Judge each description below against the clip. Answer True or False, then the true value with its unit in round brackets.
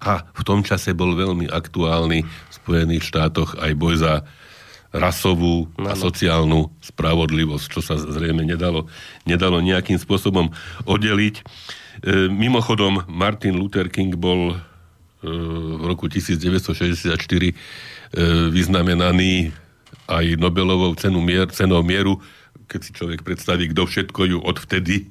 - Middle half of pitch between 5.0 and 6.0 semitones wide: False (2.5 semitones)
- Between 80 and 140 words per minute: True (120 wpm)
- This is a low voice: True (90 Hz)